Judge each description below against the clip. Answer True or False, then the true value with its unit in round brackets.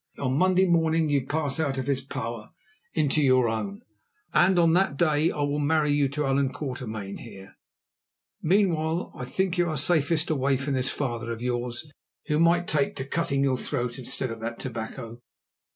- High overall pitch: False (140 Hz)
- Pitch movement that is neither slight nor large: True (4.2 semitones)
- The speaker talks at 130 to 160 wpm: False (180 wpm)